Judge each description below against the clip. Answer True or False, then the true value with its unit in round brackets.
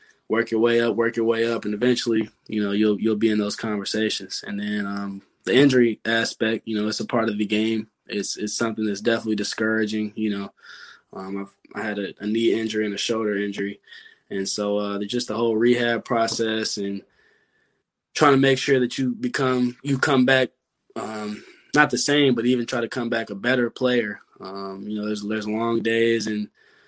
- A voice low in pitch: True (110 Hz)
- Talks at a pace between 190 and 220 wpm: True (205 wpm)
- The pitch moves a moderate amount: False (2.1 semitones)